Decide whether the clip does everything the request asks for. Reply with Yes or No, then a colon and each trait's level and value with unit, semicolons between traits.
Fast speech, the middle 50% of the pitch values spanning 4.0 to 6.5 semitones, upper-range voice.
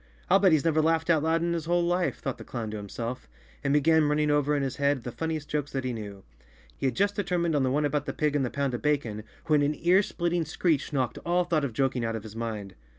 No: fast, 275 wpm; average, 4.3 semitones; medium, 145 Hz